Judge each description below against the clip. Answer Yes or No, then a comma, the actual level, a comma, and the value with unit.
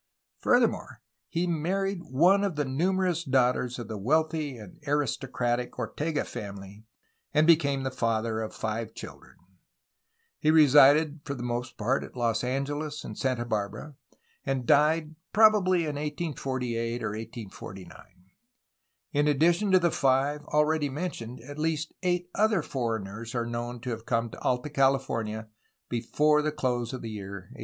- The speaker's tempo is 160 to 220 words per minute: No, average, 150 wpm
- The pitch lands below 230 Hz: Yes, low, 135 Hz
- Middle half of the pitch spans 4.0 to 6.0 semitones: Yes, average, 4.8 semitones